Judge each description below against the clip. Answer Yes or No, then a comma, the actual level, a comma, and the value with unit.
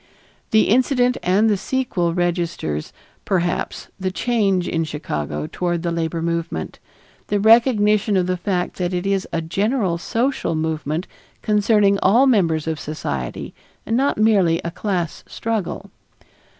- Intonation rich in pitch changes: No, average, 4.3 semitones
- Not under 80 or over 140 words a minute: Yes, slow, 135 wpm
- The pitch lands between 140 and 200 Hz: Yes, medium, 185 Hz